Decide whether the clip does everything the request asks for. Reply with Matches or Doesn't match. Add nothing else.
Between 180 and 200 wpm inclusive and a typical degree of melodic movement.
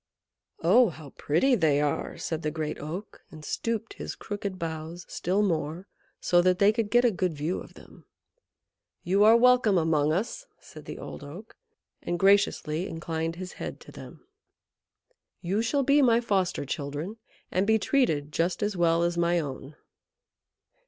Doesn't match